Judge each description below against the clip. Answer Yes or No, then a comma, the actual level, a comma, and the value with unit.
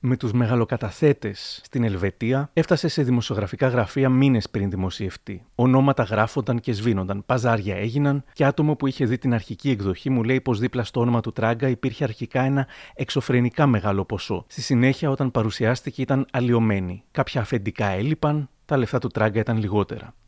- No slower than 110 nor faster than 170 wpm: Yes, average, 165 wpm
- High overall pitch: No, low, 125 Hz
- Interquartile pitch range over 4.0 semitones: No, average, 3.5 semitones